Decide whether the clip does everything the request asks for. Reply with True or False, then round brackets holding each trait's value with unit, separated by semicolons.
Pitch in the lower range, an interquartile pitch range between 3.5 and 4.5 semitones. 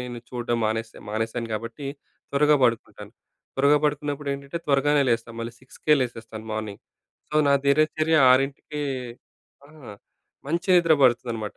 True (130 Hz; 4.2 semitones)